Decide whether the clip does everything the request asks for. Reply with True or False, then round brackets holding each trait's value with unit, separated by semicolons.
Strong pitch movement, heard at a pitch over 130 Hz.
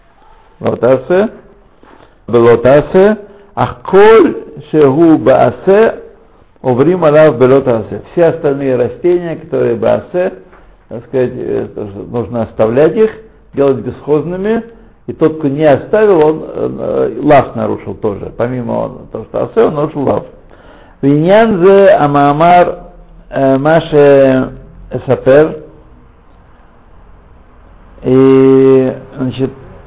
True (6.4 semitones; 140 Hz)